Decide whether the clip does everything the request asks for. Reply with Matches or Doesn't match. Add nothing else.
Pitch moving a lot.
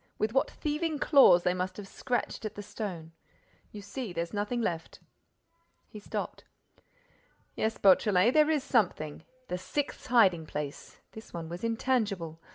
Matches